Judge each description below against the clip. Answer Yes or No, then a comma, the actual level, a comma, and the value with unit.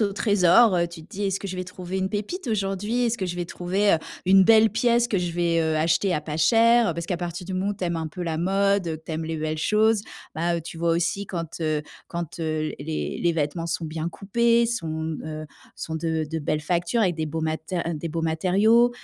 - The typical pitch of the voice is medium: Yes, medium, 175 Hz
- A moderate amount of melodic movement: Yes, average, 3.7 semitones